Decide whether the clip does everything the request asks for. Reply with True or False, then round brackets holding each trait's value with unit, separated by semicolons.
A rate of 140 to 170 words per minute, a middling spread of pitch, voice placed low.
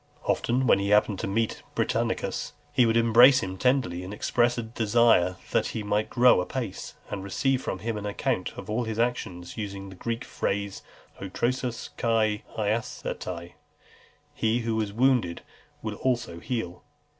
True (160 wpm; 3.5 semitones; 110 Hz)